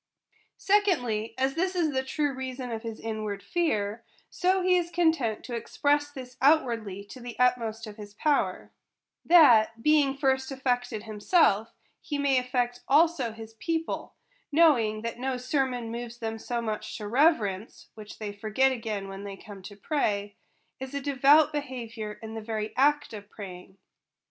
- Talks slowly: No, average, 165 wpm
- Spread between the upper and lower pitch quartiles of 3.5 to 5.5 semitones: Yes, average, 4.7 semitones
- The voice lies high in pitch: Yes, high, 245 Hz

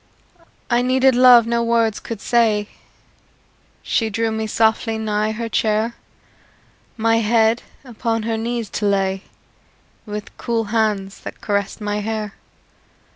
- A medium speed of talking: No, slow, 130 wpm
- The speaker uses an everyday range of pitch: No, narrow, 1.7 semitones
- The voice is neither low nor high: No, high, 220 Hz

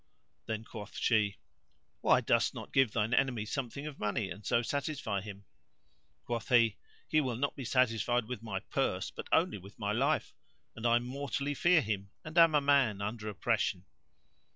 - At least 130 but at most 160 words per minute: No, average, 175 wpm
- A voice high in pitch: No, low, 115 Hz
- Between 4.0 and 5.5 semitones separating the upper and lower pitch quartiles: Yes, average, 4.6 semitones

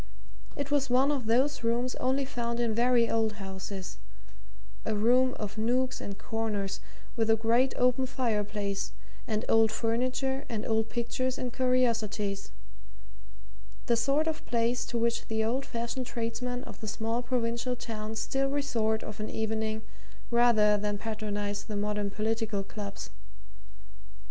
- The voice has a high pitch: Yes, high, 230 Hz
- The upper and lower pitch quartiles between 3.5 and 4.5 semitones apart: No, average, 2.7 semitones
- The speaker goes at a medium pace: Yes, average, 145 wpm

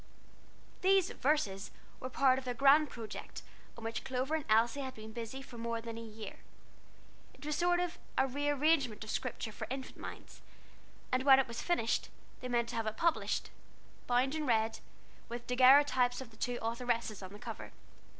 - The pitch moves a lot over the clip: No, average, 3.3 semitones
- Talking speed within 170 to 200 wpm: Yes, average, 180 wpm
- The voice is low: No, very high, 250 Hz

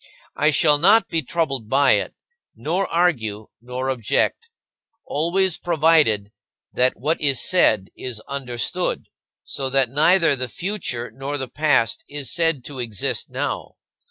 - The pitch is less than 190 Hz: Yes, medium, 140 Hz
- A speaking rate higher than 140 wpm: No, slow, 135 wpm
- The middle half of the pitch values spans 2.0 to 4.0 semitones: No, average, 4.9 semitones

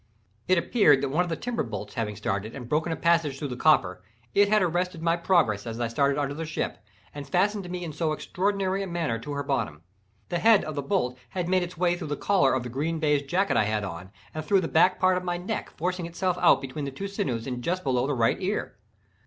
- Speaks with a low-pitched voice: No, medium, 160 Hz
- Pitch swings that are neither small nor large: No, wide, 5.8 semitones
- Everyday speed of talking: No, fast, 245 wpm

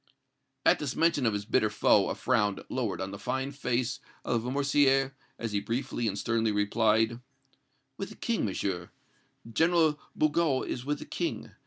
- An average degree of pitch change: Yes, average, 4.6 semitones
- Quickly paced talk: No, average, 165 wpm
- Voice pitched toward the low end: Yes, low, 120 Hz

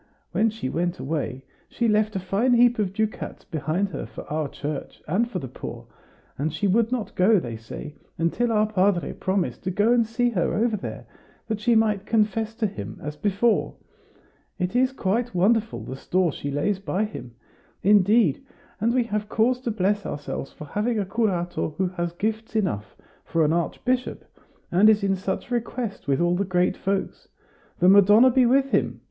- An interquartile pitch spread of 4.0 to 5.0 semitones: Yes, average, 4.3 semitones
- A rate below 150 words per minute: No, average, 185 wpm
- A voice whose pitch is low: No, high, 200 Hz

